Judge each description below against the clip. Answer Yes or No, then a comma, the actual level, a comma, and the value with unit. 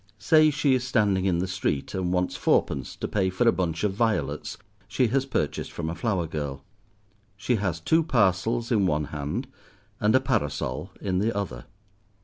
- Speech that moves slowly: No, average, 180 wpm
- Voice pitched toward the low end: Yes, very low, 95 Hz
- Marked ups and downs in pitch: Yes, wide, 5.7 semitones